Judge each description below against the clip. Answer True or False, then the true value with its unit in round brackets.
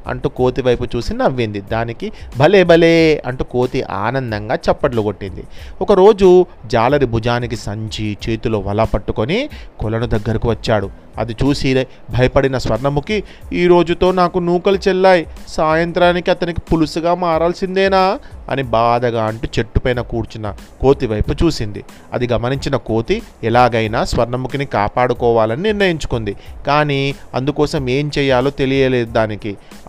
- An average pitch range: False (6.0 semitones)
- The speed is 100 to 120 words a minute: True (110 wpm)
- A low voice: True (125 Hz)